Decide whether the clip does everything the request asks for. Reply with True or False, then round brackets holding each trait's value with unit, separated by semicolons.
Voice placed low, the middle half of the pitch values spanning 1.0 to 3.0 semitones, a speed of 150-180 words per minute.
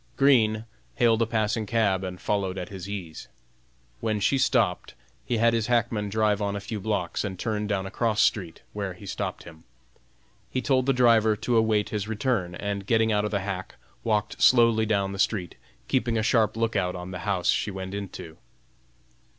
False (105 Hz; 2.7 semitones; 190 wpm)